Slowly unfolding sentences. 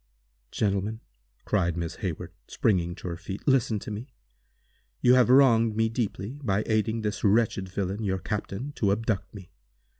No: average, 155 wpm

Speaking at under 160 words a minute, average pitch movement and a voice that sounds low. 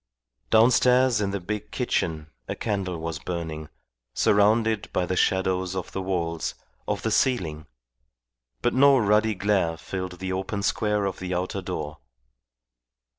Yes: average, 140 wpm; average, 3.4 semitones; very low, 95 Hz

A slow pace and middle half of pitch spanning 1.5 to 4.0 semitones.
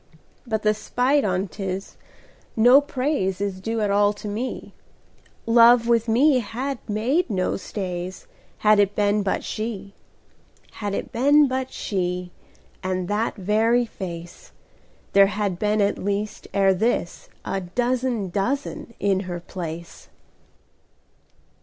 Yes: slow, 120 wpm; average, 3.7 semitones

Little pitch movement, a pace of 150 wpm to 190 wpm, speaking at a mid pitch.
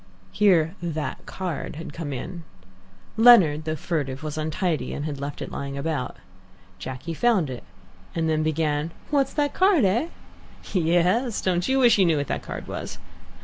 No: average, 4.3 semitones; average, 160 wpm; medium, 165 Hz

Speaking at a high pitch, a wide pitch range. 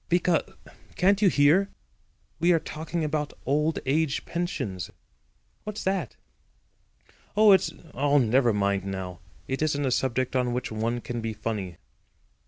No: medium, 140 Hz; wide, 6.5 semitones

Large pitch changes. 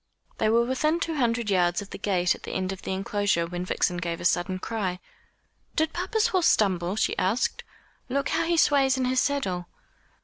Yes: wide, 7.1 semitones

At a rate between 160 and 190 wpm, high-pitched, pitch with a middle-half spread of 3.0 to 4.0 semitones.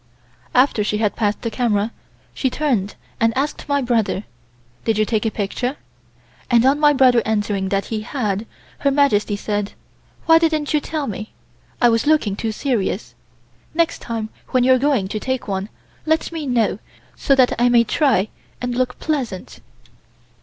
No: average, 170 wpm; high, 235 Hz; average, 4.6 semitones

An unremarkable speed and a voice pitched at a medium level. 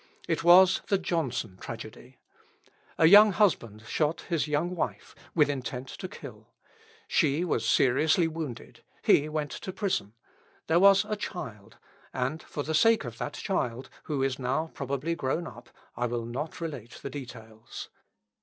Yes: average, 155 wpm; medium, 145 Hz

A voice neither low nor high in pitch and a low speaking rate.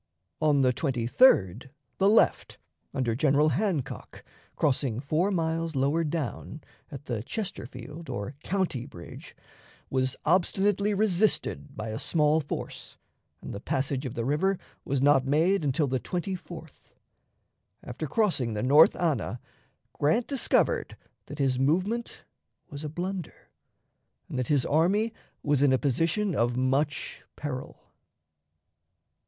Yes: medium, 150 Hz; slow, 125 wpm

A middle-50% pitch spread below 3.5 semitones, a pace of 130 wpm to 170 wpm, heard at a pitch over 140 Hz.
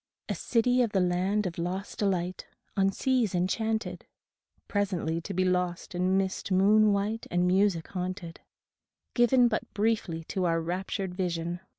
Yes: average, 2.8 semitones; average, 150 wpm; high, 190 Hz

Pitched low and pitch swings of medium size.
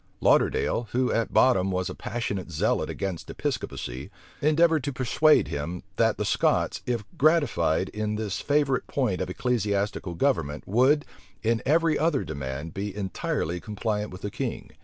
No: low, 105 Hz; wide, 6.4 semitones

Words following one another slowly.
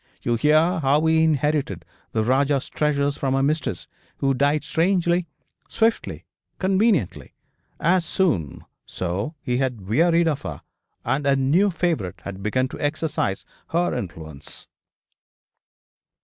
Yes: slow, 125 wpm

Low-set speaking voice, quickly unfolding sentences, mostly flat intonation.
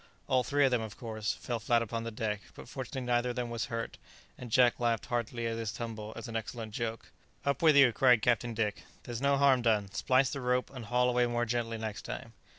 Yes: low, 120 Hz; fast, 235 wpm; narrow, 1.7 semitones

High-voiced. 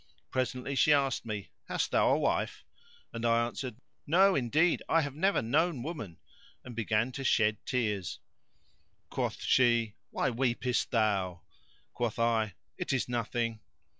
No: low, 120 Hz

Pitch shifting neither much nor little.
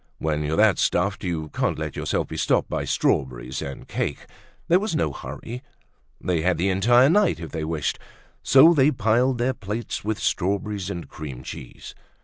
No: wide, 7.4 semitones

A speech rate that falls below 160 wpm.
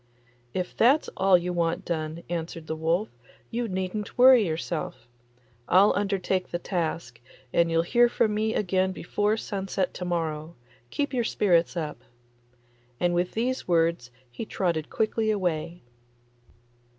Yes: average, 140 wpm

